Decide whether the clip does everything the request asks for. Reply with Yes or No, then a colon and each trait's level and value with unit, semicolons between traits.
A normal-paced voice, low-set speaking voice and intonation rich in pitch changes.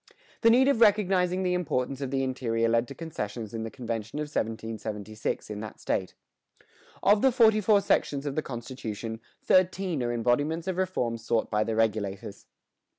Yes: average, 170 wpm; low, 130 Hz; wide, 8.2 semitones